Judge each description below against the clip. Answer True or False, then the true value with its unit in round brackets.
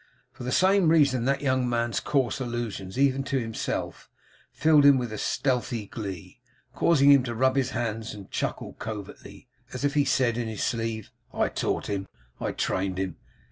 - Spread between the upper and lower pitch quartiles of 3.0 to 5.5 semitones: True (3.8 semitones)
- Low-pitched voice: True (120 Hz)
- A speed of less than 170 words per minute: False (180 wpm)